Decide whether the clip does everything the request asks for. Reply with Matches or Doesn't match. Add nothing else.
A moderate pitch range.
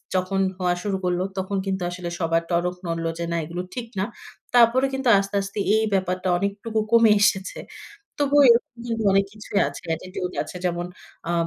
Matches